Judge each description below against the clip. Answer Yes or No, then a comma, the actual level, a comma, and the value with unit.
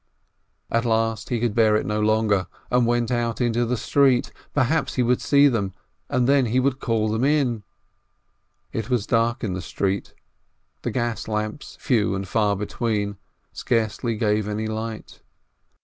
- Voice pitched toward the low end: Yes, low, 115 Hz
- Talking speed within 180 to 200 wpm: No, average, 165 wpm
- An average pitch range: No, narrow, 2.3 semitones